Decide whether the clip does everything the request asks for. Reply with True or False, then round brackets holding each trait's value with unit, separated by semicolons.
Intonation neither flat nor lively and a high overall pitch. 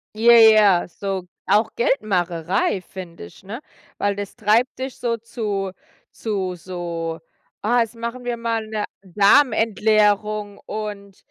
True (3.2 semitones; 210 Hz)